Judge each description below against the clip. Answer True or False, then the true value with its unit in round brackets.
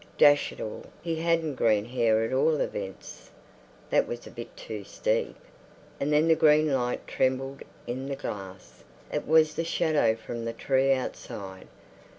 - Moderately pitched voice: False (130 Hz)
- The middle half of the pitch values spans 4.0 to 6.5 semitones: True (5.1 semitones)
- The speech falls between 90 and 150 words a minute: False (160 wpm)